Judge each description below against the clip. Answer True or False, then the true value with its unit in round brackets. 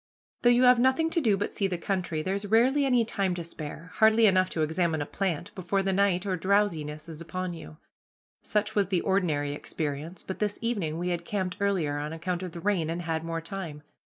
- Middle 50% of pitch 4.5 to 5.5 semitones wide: False (3.8 semitones)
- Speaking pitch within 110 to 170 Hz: False (185 Hz)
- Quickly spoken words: True (215 wpm)